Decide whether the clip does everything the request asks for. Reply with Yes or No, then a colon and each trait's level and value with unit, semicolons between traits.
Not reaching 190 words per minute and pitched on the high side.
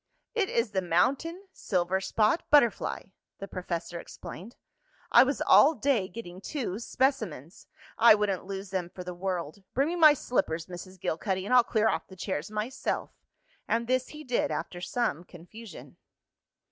Yes: average, 155 wpm; high, 205 Hz